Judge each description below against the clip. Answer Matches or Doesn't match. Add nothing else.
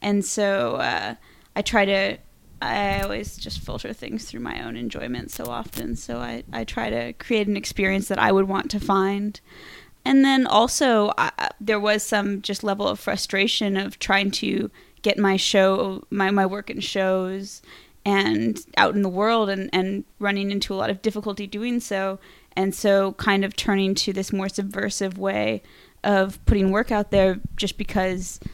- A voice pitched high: Matches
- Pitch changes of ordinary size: Doesn't match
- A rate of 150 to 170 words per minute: Doesn't match